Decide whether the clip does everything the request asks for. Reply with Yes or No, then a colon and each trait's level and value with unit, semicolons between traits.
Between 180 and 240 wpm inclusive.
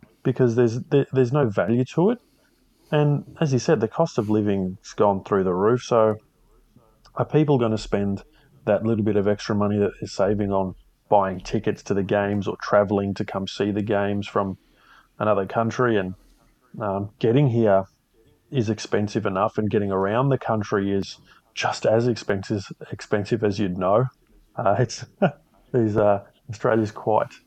No: average, 170 wpm